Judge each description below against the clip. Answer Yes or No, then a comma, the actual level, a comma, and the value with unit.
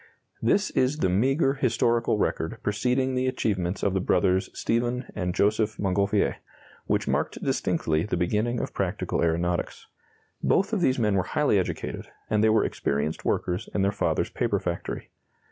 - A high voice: No, low, 105 Hz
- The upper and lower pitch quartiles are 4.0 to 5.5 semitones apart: Yes, average, 5.1 semitones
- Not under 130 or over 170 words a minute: Yes, average, 160 wpm